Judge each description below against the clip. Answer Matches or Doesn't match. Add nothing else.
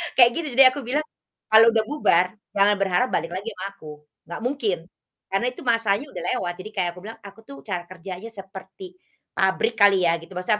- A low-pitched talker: Doesn't match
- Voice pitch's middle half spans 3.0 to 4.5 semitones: Matches